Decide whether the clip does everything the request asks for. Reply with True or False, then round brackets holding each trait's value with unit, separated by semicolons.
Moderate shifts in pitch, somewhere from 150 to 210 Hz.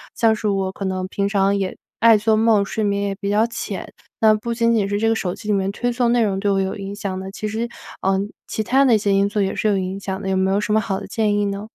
False (2.0 semitones; 205 Hz)